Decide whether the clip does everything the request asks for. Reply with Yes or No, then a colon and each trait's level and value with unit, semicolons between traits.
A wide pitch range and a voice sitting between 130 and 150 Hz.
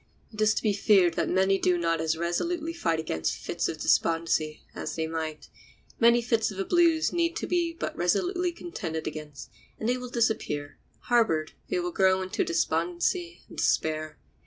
No: wide, 7.7 semitones; high, 190 Hz